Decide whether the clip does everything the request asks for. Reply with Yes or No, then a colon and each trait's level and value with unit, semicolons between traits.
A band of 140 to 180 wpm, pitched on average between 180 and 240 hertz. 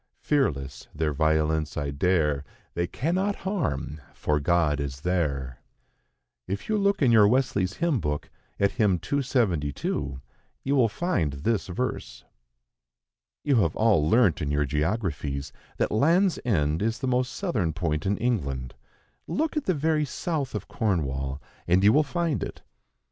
No: average, 150 wpm; very low, 95 Hz